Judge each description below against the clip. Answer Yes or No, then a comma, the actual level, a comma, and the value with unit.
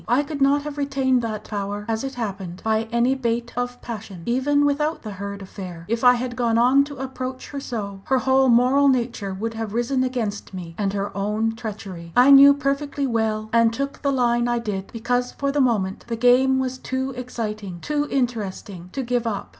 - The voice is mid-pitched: No, high, 240 Hz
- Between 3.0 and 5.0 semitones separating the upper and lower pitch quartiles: Yes, average, 3.7 semitones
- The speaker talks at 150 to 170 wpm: No, fast, 205 wpm